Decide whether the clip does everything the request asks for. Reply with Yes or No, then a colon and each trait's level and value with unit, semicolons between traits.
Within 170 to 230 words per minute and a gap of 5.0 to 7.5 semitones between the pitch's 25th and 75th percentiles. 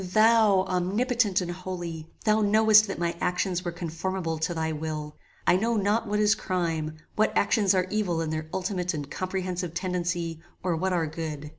No: average, 175 wpm; average, 3.6 semitones